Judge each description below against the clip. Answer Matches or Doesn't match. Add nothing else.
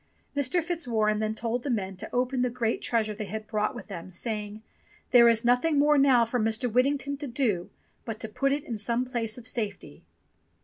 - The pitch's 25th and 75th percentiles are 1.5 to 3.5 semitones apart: Matches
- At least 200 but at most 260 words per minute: Matches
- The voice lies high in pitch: Matches